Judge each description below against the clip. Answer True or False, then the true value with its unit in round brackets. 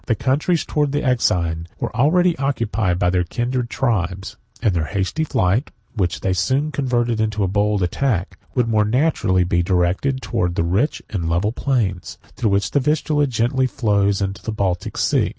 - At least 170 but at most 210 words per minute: True (175 wpm)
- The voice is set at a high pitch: False (110 Hz)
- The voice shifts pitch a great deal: True (6.0 semitones)